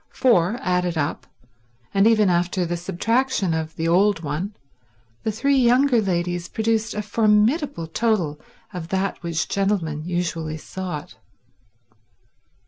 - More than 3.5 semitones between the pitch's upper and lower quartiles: Yes, average, 4.5 semitones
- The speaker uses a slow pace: Yes, slow, 125 wpm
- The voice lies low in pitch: No, medium, 185 Hz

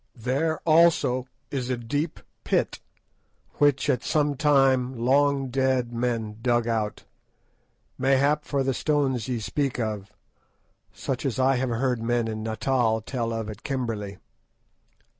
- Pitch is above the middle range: No, low, 125 Hz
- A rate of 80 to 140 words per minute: Yes, slow, 135 wpm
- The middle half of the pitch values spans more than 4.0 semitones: No, average, 3.1 semitones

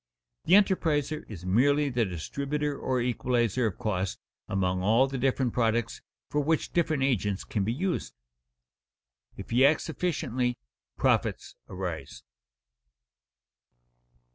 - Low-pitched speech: Yes, low, 125 Hz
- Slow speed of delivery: Yes, slow, 115 wpm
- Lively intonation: Yes, wide, 6.0 semitones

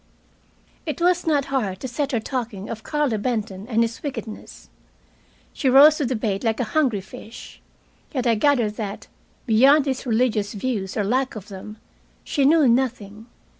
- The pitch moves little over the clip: No, average, 4.3 semitones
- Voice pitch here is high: Yes, high, 240 Hz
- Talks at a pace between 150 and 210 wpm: Yes, average, 170 wpm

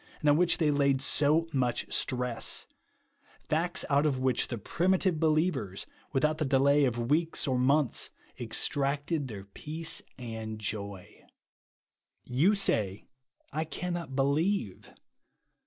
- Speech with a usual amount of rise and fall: Yes, average, 4.3 semitones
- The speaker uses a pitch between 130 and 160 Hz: Yes, medium, 140 Hz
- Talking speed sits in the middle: No, slow, 125 wpm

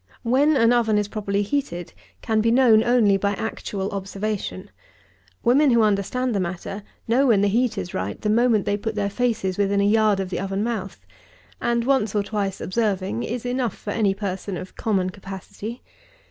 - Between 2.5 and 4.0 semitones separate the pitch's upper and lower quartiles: Yes, average, 3.1 semitones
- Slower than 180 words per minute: No, average, 185 wpm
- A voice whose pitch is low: No, high, 210 Hz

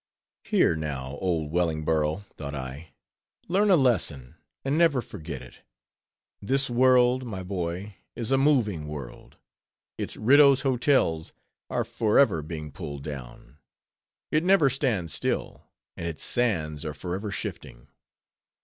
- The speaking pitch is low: Yes, very low, 90 Hz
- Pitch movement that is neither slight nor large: No, wide, 9.0 semitones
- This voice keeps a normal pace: No, slow, 125 wpm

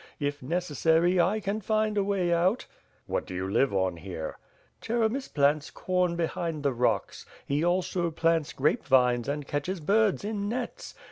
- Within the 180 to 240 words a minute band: No, average, 160 wpm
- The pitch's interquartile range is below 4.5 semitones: No, wide, 5.6 semitones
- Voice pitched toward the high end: No, medium, 170 Hz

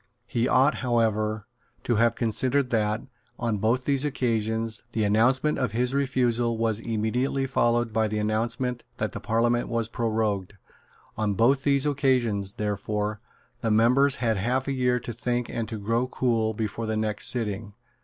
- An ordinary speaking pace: Yes, average, 160 wpm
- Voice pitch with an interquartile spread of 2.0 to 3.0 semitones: Yes, narrow, 2.6 semitones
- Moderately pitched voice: No, low, 115 Hz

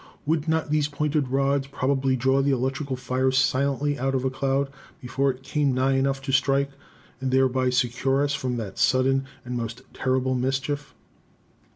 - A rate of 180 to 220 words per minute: No, average, 170 wpm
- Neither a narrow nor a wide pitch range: No, narrow, 1.3 semitones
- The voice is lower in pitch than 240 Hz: Yes, low, 135 Hz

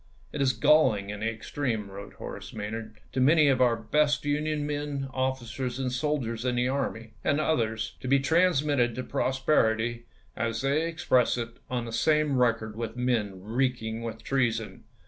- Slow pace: No, average, 185 wpm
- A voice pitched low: Yes, low, 125 Hz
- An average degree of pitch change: Yes, average, 3.8 semitones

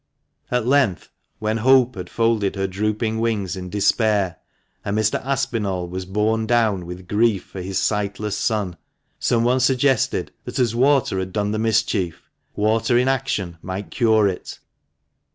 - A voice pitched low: Yes, low, 110 Hz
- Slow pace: No, average, 150 wpm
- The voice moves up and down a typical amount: Yes, average, 3.3 semitones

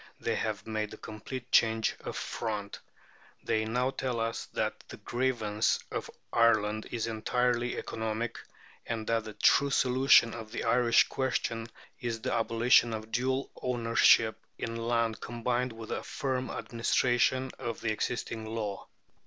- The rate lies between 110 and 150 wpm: Yes, average, 145 wpm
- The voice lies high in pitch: No, low, 115 Hz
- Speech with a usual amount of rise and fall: No, narrow, 1.9 semitones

